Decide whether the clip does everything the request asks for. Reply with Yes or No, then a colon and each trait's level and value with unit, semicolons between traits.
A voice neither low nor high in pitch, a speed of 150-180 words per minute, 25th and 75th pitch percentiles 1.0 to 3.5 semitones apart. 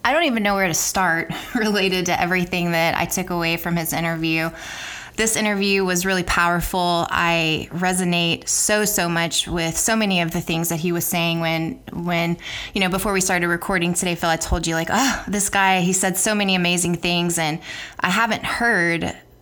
No: medium, 175 Hz; average, 200 wpm; narrow, 2.4 semitones